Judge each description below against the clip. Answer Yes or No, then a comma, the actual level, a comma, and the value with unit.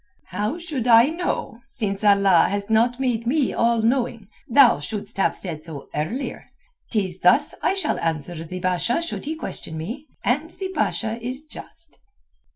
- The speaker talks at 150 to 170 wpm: Yes, average, 160 wpm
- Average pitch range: No, wide, 6.4 semitones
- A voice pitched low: No, high, 230 Hz